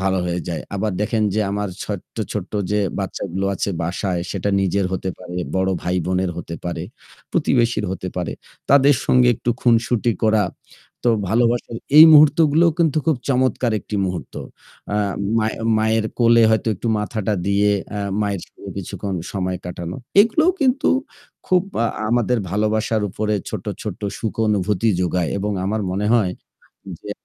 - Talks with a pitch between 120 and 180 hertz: No, low, 105 Hz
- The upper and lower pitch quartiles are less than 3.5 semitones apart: No, average, 3.9 semitones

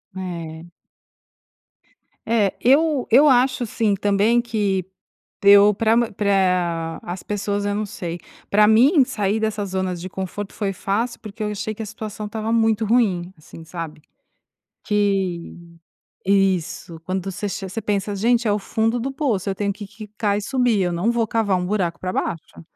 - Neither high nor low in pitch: No, high, 205 Hz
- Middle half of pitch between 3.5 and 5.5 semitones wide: No, average, 2.9 semitones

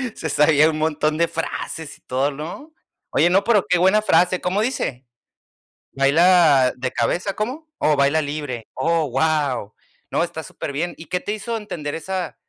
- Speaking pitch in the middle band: Yes, medium, 160 Hz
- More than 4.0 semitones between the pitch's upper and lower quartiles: Yes, average, 4.4 semitones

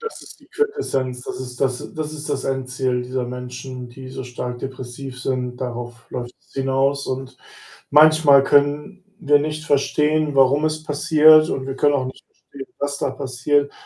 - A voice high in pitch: No, low, 135 Hz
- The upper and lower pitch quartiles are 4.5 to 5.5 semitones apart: No, average, 2.7 semitones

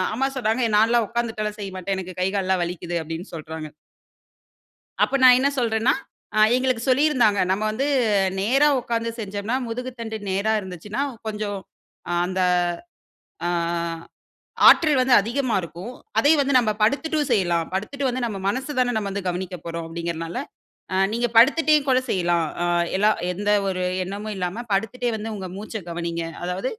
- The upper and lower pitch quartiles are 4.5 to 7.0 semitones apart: Yes, average, 5.0 semitones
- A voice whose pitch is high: Yes, high, 215 Hz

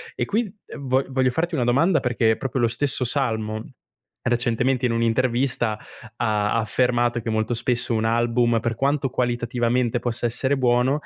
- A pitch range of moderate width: No, narrow, 2.1 semitones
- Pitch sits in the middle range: No, low, 120 Hz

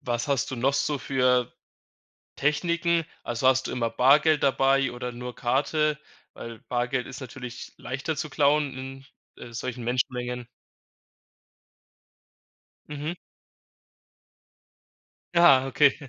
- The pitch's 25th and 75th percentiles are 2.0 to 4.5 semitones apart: Yes, average, 2.9 semitones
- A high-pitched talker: No, low, 130 Hz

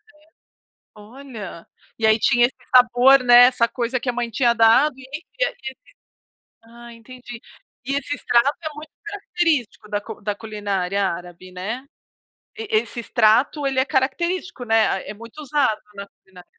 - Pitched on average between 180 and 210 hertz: No, high, 240 Hz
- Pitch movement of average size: Yes, average, 4.1 semitones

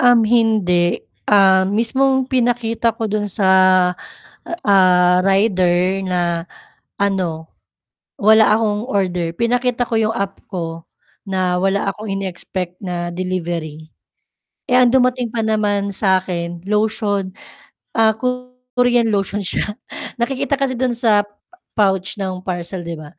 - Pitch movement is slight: No, average, 4.0 semitones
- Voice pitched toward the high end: Yes, high, 200 Hz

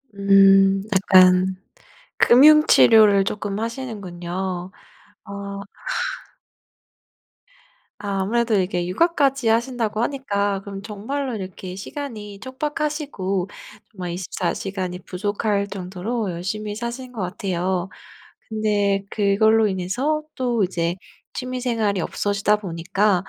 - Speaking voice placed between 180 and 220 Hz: Yes, high, 200 Hz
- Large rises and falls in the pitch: No, average, 3.6 semitones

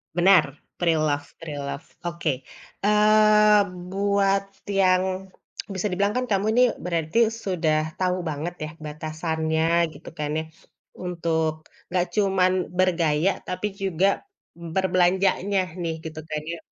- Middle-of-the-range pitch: Yes, medium, 180 Hz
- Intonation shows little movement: No, average, 3.6 semitones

